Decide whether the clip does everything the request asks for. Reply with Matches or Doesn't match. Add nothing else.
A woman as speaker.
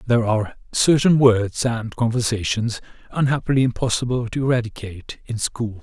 Doesn't match